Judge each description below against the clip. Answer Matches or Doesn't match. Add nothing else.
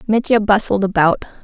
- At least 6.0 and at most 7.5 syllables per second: Doesn't match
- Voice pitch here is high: Matches